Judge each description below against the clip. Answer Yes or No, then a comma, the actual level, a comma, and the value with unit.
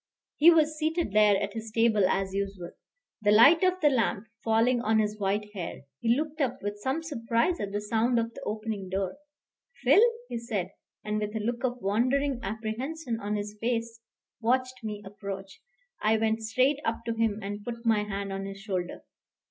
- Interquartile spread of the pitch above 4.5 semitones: No, average, 3.0 semitones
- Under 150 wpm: No, average, 190 wpm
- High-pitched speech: Yes, high, 220 Hz